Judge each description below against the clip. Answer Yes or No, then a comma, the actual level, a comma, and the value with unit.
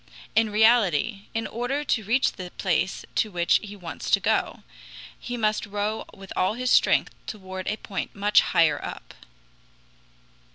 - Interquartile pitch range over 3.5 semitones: No, average, 3.1 semitones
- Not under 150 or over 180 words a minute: Yes, average, 155 wpm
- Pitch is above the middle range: Yes, high, 210 Hz